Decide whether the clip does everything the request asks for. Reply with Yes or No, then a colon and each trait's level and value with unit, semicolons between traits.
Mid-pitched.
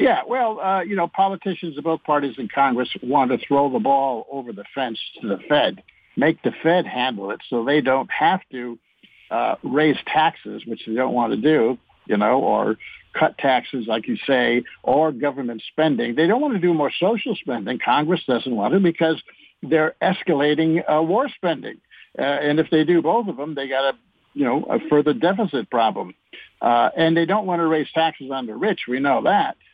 Yes: medium, 155 Hz